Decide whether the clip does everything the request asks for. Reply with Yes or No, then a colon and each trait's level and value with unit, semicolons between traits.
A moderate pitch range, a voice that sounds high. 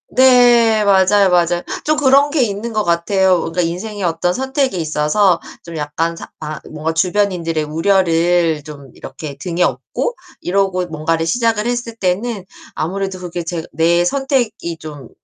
No: average, 4.5 semitones; medium, 180 Hz